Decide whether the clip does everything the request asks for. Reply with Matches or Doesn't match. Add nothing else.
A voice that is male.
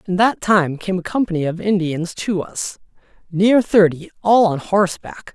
Matches